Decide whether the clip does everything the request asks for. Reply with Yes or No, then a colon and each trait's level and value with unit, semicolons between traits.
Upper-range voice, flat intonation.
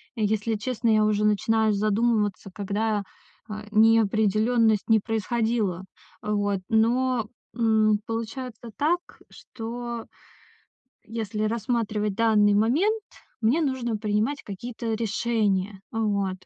Yes: high, 220 Hz; narrow, 1.9 semitones